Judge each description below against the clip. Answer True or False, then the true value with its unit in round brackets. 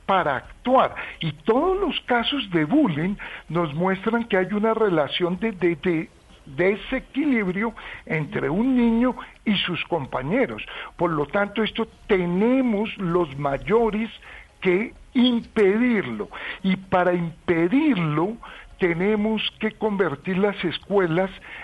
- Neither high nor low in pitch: False (200 Hz)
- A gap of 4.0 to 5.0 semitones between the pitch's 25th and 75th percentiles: True (4.4 semitones)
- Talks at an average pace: False (115 wpm)